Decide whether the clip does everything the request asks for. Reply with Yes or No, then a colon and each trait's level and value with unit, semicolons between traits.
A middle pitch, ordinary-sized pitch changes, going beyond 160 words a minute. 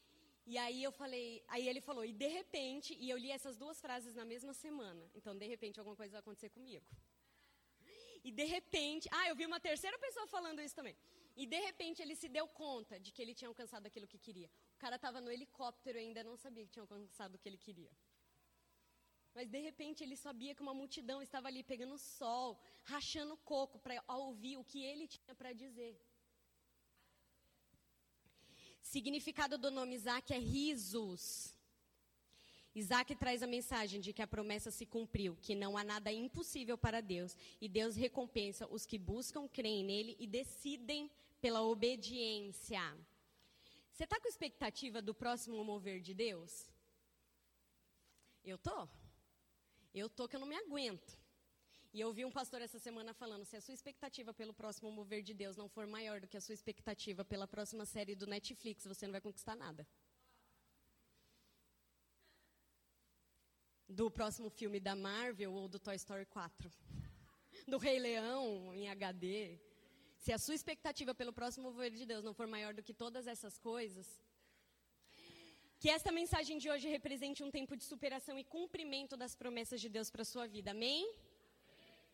No: high, 235 Hz; average, 4.7 semitones; average, 170 wpm